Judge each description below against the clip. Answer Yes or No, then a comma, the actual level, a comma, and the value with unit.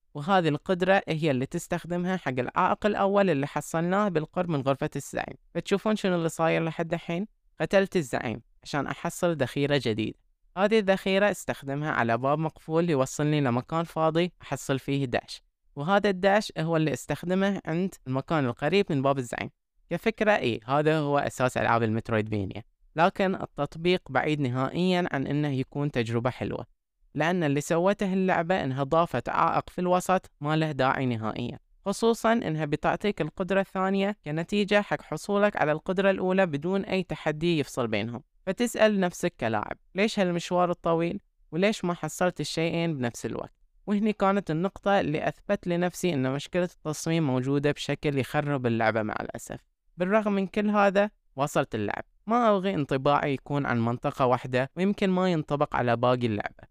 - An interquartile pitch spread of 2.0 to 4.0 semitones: No, wide, 5.4 semitones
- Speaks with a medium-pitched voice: Yes, medium, 160 Hz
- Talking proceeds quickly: Yes, fast, 150 wpm